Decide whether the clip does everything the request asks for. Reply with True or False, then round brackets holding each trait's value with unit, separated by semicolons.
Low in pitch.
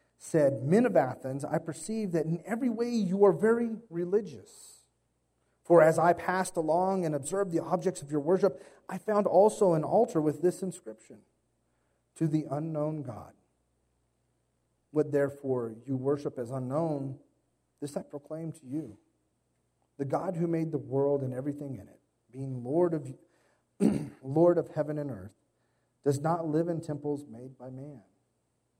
False (150 Hz)